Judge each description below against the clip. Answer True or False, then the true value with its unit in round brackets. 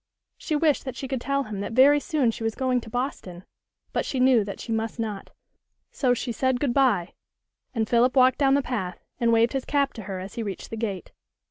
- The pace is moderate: False (230 wpm)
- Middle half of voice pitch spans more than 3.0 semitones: True (3.4 semitones)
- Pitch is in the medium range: False (245 Hz)